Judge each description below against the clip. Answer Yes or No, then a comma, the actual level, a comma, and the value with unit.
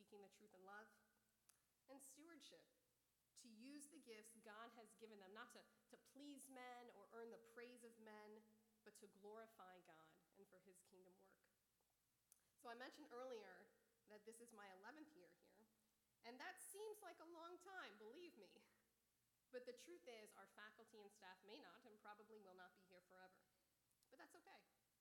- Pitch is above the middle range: Yes, high, 225 Hz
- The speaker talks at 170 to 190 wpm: Yes, average, 180 wpm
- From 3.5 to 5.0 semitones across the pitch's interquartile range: Yes, average, 4.6 semitones